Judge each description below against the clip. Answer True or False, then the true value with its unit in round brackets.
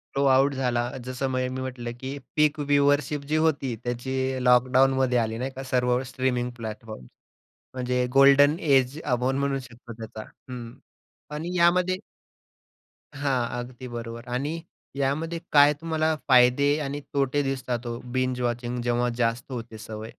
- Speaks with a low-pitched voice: True (130 Hz)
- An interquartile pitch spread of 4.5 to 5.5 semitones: False (2.6 semitones)